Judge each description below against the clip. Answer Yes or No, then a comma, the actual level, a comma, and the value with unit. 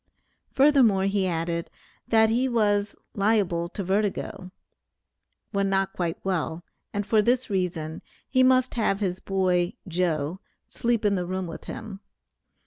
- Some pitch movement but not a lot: Yes, average, 3.6 semitones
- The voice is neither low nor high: No, high, 195 Hz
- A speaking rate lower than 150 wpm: Yes, slow, 135 wpm